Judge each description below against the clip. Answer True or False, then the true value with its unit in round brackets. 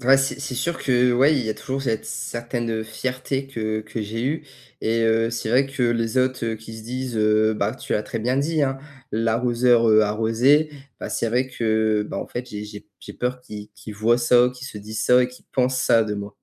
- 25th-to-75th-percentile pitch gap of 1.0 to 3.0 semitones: True (2.6 semitones)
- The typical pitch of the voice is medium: False (120 Hz)